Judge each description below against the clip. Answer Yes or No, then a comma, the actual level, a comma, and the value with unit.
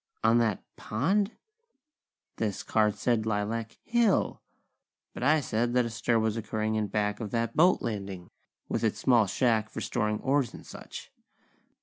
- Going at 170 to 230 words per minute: No, average, 155 wpm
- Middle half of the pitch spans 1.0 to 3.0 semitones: Yes, narrow, 2.4 semitones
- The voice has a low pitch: Yes, low, 115 Hz